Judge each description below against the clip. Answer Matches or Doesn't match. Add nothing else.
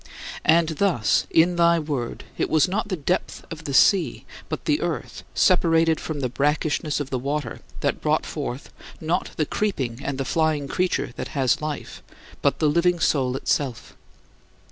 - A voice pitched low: Doesn't match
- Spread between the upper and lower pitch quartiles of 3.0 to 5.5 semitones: Matches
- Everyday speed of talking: Matches